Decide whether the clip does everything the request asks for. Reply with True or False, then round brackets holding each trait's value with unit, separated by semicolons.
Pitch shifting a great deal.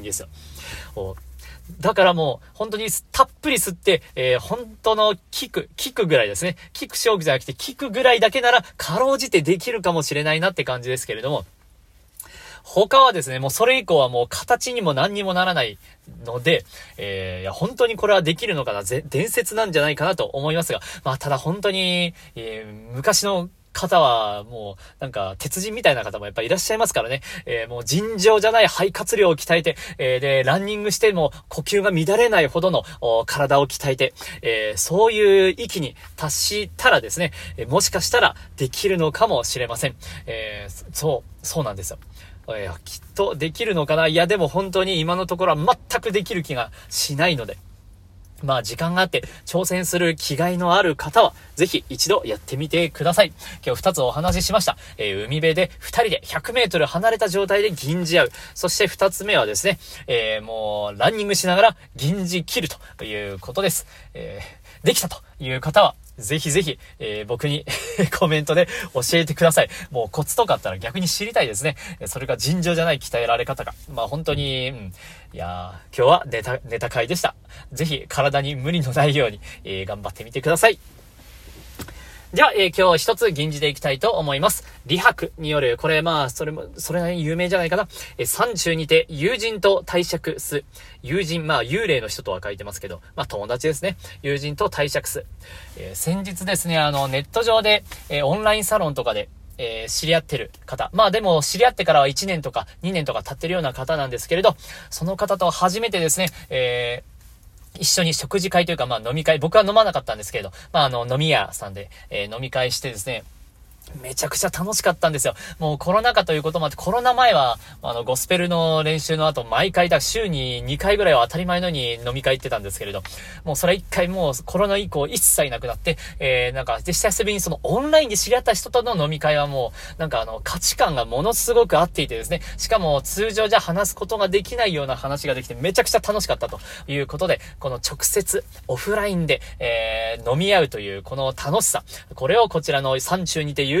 True (7.1 semitones)